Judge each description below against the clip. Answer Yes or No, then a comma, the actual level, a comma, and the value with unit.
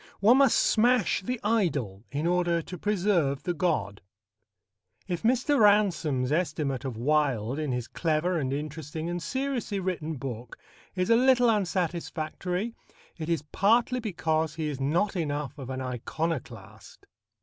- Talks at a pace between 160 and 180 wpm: No, average, 140 wpm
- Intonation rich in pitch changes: Yes, wide, 6.2 semitones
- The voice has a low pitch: No, medium, 165 Hz